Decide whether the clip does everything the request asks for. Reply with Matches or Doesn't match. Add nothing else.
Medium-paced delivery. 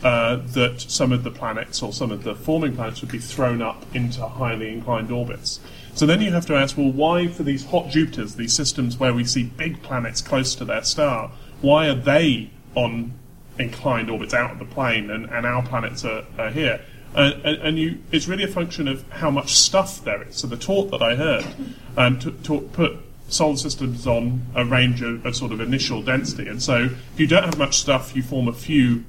Doesn't match